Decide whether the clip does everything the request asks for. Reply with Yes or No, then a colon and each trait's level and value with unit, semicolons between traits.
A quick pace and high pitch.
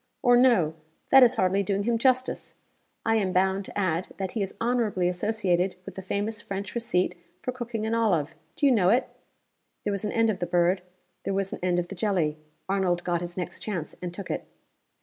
Yes: fast, 210 wpm; high, 195 Hz